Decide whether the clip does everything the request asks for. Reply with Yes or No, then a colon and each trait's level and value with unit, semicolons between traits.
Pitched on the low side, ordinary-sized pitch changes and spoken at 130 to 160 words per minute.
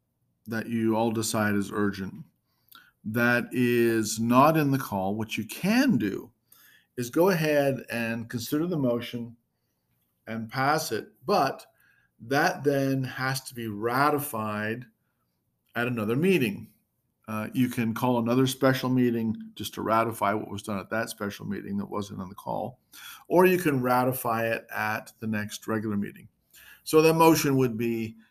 Yes: low, 120 Hz; average, 3.1 semitones; average, 155 wpm